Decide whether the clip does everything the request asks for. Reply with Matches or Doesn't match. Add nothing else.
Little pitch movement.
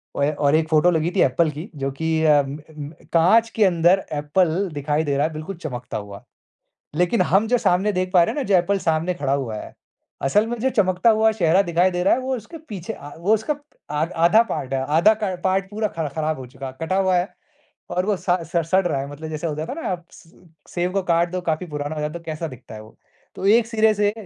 Doesn't match